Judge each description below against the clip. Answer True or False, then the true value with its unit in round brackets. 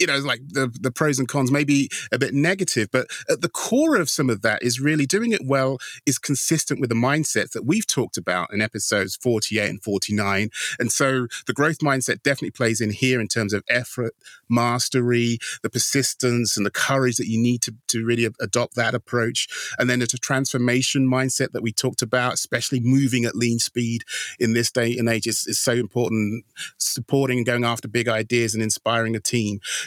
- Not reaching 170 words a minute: False (205 wpm)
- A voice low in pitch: True (120 Hz)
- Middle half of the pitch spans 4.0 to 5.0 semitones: False (2.8 semitones)